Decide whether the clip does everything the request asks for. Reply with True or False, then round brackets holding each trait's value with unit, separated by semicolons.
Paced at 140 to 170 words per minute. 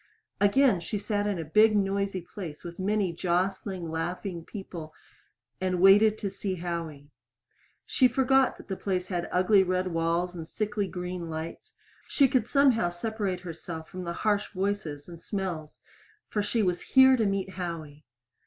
True (155 wpm)